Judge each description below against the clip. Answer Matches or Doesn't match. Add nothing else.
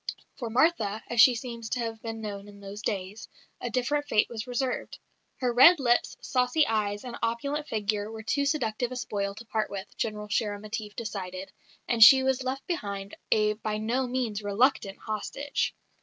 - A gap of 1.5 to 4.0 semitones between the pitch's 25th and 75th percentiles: Matches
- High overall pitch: Matches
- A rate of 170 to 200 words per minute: Matches